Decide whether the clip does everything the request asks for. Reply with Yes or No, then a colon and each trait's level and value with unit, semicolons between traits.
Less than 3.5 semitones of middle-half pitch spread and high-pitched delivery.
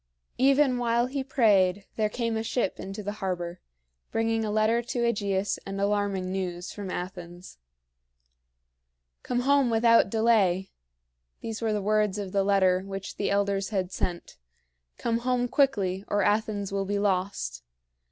Yes: average, 3.1 semitones; high, 205 Hz